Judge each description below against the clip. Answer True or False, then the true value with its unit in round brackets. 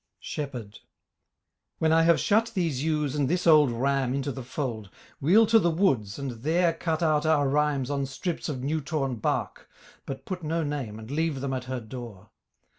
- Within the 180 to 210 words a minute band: True (190 wpm)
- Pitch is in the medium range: True (145 Hz)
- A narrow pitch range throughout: False (3.8 semitones)